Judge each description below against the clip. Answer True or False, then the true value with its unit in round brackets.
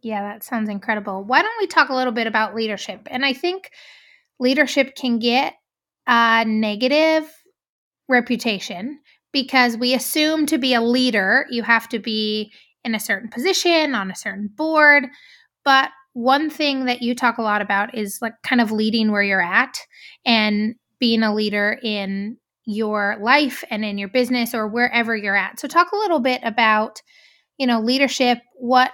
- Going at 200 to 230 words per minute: False (170 wpm)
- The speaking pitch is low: False (240 Hz)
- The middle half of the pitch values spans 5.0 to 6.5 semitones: False (3.7 semitones)